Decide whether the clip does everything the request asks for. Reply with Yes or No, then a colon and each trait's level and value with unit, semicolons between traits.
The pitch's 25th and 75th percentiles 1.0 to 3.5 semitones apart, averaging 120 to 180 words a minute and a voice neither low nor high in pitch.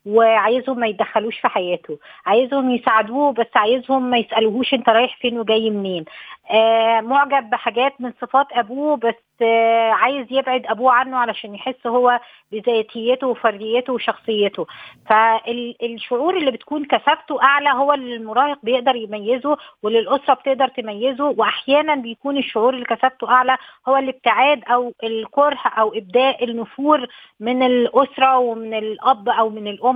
No: average, 2.8 semitones; average, 130 wpm; high, 245 Hz